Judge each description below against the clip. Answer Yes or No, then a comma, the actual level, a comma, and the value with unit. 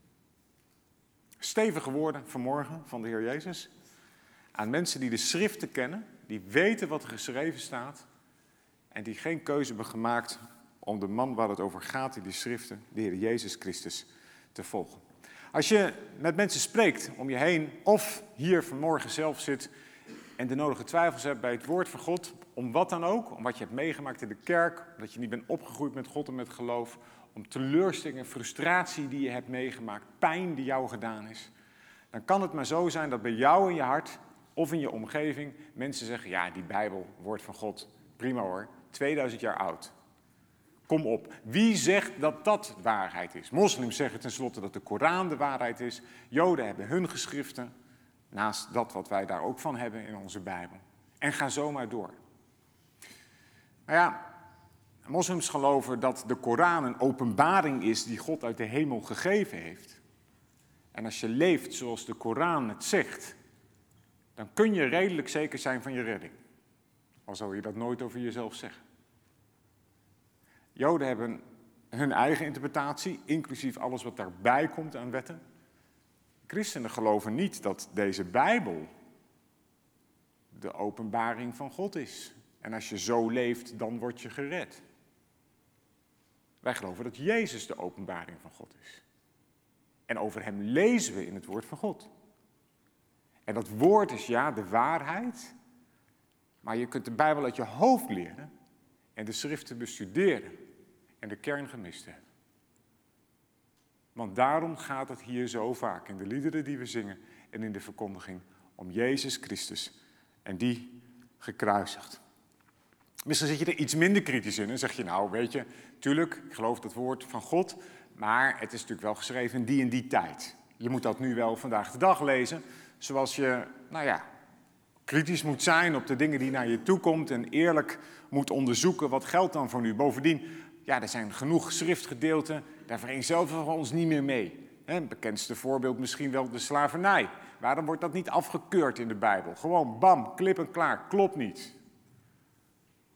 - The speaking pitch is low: Yes, low, 130 Hz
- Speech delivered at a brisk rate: No, average, 170 wpm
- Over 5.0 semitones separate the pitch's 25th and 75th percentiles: Yes, wide, 5.6 semitones